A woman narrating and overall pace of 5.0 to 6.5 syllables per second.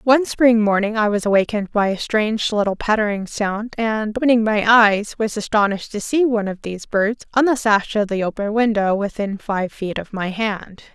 Yes: female; 5.3 syllables/s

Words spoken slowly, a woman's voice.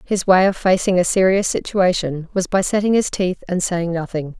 No: fast, 205 wpm; female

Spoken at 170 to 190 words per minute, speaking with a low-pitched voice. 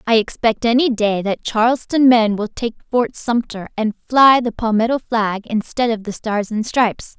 No: average, 185 wpm; high, 230 Hz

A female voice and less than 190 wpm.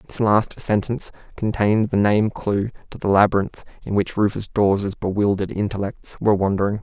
No: male; average, 160 wpm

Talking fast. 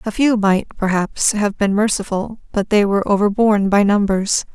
No: average, 170 wpm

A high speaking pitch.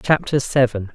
No: low, 130 Hz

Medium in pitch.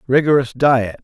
No: low, 130 Hz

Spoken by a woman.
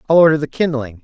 No: male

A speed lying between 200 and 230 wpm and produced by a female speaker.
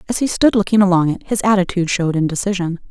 Yes: fast, 205 wpm; female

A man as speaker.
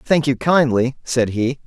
Yes: male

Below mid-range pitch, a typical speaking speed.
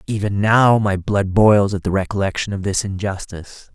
Yes: low, 100 Hz; average, 175 wpm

